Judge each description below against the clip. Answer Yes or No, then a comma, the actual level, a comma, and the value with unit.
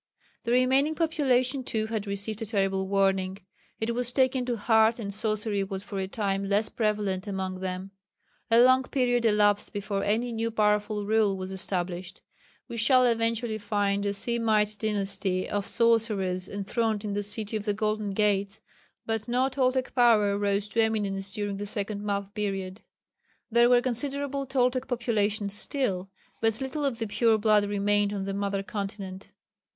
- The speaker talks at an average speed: Yes, average, 165 wpm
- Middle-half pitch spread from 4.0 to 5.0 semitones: No, average, 2.8 semitones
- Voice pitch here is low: No, high, 210 Hz